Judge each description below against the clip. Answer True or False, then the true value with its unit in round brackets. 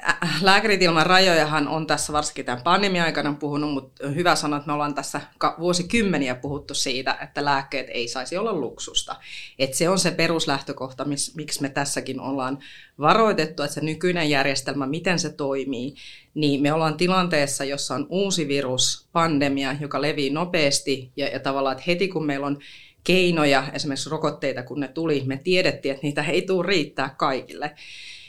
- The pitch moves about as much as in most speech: True (3.1 semitones)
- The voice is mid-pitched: True (145 Hz)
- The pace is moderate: False (165 wpm)